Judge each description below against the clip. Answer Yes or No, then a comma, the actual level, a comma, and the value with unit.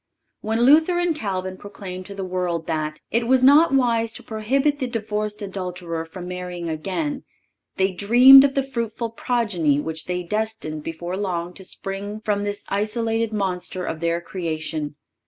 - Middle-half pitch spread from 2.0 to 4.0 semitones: No, average, 4.5 semitones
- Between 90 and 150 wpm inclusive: No, average, 165 wpm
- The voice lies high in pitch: Yes, high, 200 Hz